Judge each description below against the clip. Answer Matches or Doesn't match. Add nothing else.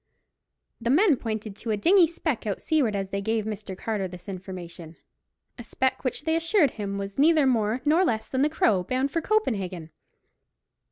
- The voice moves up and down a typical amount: Doesn't match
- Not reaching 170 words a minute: Doesn't match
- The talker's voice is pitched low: Doesn't match